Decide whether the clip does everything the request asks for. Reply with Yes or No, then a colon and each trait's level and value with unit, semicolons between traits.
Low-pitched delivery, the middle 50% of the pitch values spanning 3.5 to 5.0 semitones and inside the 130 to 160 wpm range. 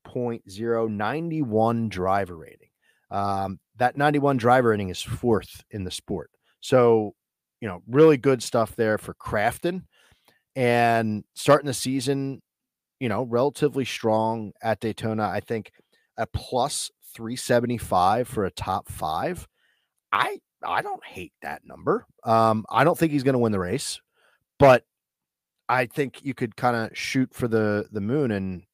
Yes: low, 115 Hz; average, 3.9 semitones; average, 150 wpm